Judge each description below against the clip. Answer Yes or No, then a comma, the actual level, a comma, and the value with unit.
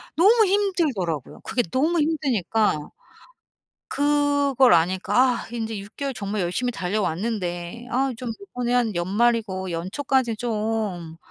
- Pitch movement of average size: No, wide, 6.3 semitones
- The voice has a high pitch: Yes, high, 230 Hz